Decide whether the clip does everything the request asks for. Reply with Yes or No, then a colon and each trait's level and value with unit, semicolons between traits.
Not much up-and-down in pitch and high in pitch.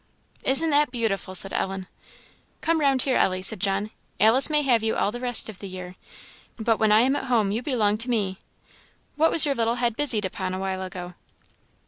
No: average, 5.1 semitones; high, 225 Hz